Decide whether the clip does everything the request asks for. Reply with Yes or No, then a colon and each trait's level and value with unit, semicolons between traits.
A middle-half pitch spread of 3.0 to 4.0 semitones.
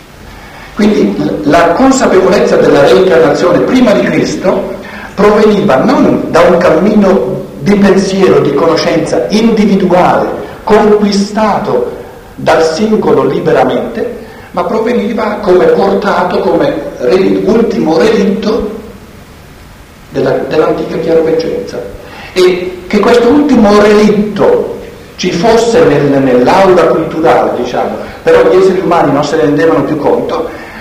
No: average, 4.9 semitones